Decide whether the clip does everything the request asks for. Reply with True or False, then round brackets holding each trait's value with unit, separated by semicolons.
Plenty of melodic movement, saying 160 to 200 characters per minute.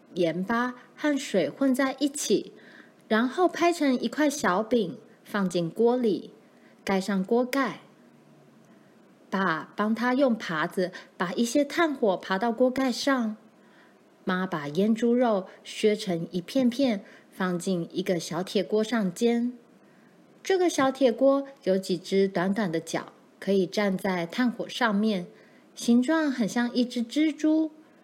True (5.8 semitones; 185 characters per minute)